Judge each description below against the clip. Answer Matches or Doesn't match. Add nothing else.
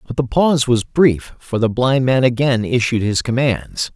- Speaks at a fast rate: Doesn't match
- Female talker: Doesn't match